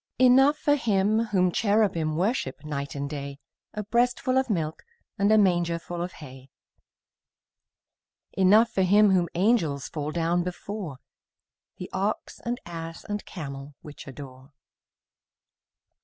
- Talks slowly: Yes, slow, 125 wpm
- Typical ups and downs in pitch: No, wide, 5.7 semitones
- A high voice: No, medium, 180 Hz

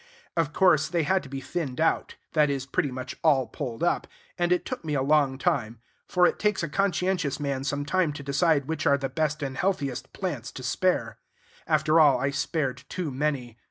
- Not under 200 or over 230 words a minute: Yes, fast, 205 wpm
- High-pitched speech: No, medium, 145 Hz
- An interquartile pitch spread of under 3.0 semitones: No, average, 3.9 semitones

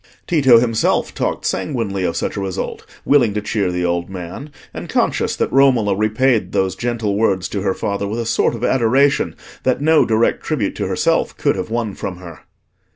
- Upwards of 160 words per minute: Yes, average, 190 wpm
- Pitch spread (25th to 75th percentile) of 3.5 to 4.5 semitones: Yes, average, 4.1 semitones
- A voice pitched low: Yes, low, 110 Hz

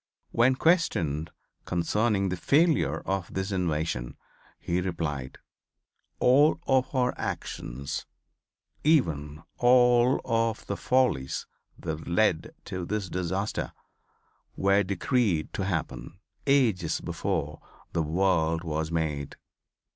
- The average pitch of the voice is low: Yes, very low, 95 Hz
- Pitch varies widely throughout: Yes, wide, 6.9 semitones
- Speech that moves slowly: Yes, slow, 100 wpm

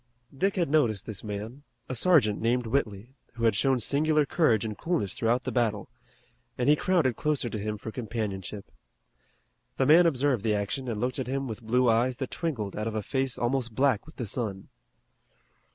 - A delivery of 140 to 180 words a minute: No, average, 190 wpm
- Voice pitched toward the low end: Yes, low, 120 Hz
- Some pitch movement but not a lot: Yes, average, 4.1 semitones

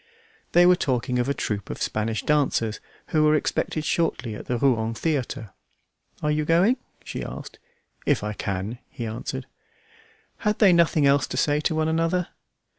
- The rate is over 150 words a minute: Yes, average, 170 wpm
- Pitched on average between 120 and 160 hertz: Yes, medium, 140 Hz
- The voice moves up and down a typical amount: No, wide, 5.7 semitones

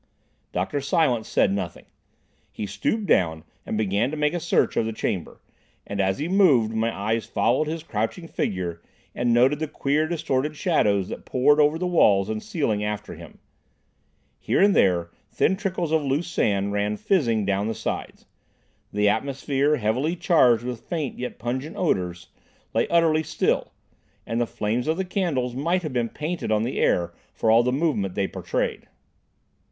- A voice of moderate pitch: No, low, 125 Hz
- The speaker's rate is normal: Yes, average, 170 wpm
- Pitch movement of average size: No, wide, 7.0 semitones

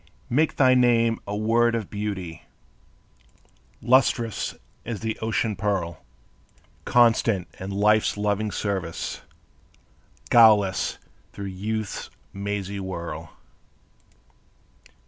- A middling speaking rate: No, slow, 90 wpm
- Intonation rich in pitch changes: No, average, 2.8 semitones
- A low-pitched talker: Yes, low, 105 Hz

